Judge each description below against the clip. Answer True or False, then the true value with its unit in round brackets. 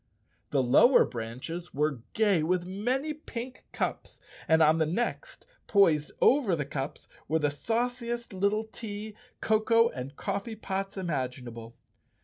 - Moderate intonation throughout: False (7.4 semitones)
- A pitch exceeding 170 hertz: True (190 Hz)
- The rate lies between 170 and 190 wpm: False (135 wpm)